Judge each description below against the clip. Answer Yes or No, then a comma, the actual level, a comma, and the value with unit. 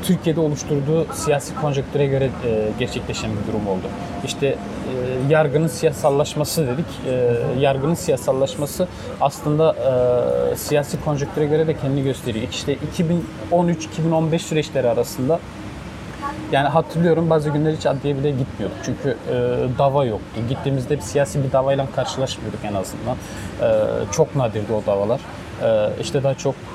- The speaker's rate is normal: Yes, average, 130 wpm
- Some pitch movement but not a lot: Yes, average, 3.9 semitones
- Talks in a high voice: No, medium, 140 Hz